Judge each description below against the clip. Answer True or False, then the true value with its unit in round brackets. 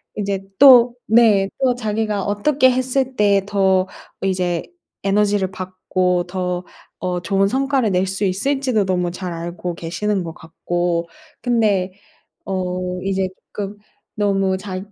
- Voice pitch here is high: True (195 Hz)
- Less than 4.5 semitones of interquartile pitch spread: True (2.7 semitones)